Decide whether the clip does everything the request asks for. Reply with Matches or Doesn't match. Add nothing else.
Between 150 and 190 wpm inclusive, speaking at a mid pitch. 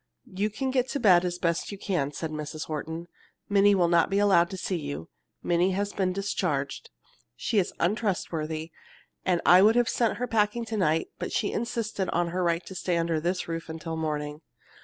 Doesn't match